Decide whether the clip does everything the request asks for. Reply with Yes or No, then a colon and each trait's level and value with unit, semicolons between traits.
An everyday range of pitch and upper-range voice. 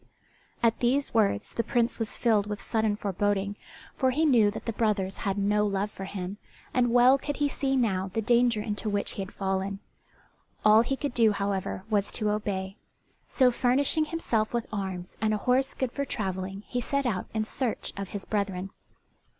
Yes: average, 3.6 semitones; high, 215 Hz